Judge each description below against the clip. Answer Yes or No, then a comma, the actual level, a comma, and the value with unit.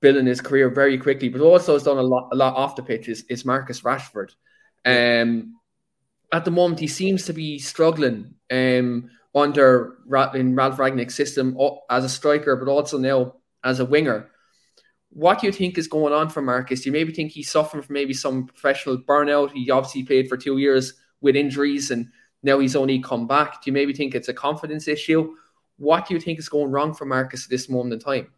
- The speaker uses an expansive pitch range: No, narrow, 2.5 semitones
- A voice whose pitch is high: No, medium, 140 Hz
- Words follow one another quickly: Yes, fast, 210 wpm